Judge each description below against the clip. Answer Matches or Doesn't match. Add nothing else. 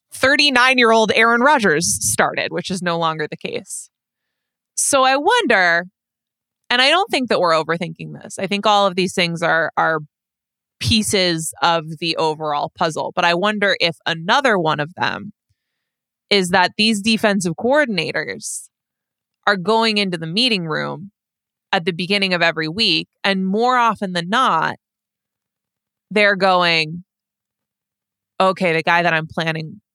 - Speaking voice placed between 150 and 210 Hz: Matches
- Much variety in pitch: Doesn't match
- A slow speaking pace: Doesn't match